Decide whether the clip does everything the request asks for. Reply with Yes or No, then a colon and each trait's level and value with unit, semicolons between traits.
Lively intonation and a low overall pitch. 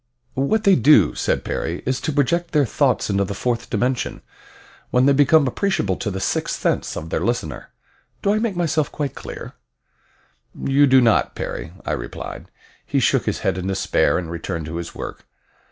Yes: wide, 7.7 semitones; low, 130 Hz